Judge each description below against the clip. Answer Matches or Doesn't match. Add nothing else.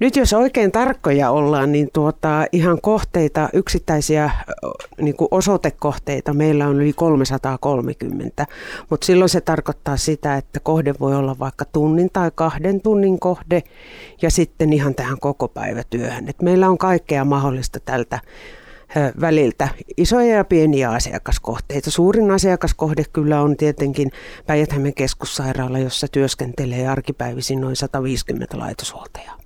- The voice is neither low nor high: Matches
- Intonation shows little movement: Doesn't match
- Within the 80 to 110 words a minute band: Doesn't match